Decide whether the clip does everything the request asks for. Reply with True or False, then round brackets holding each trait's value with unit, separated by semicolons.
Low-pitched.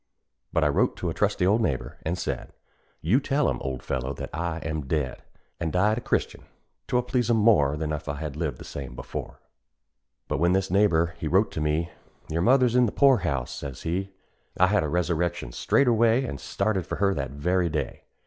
True (85 Hz)